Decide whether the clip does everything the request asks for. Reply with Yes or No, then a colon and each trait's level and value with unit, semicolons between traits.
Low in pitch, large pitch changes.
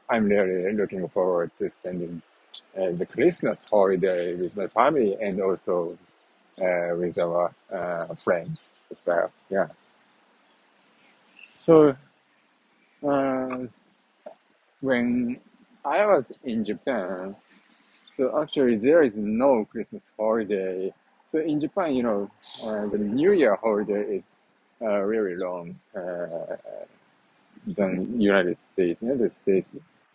Yes: low, 115 Hz; wide, 8.5 semitones